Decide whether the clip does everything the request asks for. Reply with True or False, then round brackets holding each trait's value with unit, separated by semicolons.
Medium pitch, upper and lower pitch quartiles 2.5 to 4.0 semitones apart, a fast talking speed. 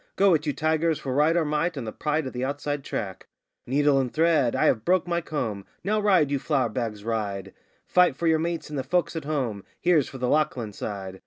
False (145 Hz; 4.8 semitones; 230 wpm)